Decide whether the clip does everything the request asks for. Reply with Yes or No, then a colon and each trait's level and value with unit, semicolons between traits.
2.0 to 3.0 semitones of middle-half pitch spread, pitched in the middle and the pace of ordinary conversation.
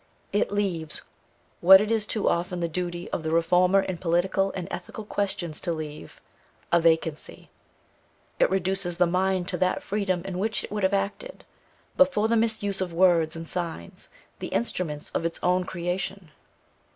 Yes: narrow, 2.5 semitones; medium, 180 Hz; average, 170 wpm